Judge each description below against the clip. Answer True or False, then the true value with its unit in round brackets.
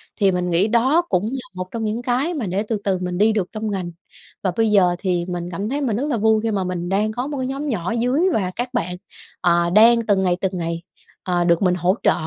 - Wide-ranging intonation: False (4.6 semitones)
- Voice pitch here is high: True (200 Hz)